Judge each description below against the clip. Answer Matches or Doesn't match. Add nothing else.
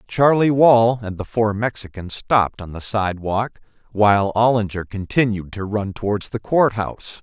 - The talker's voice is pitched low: Matches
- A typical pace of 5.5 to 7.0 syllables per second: Doesn't match